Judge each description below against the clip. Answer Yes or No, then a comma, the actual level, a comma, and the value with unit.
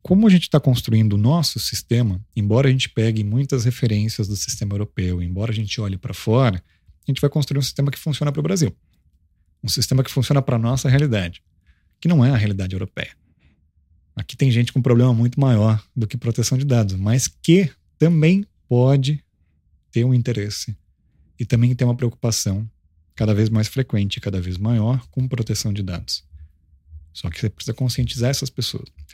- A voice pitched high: No, low, 115 Hz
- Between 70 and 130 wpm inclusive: No, fast, 185 wpm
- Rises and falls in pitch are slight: No, wide, 5.6 semitones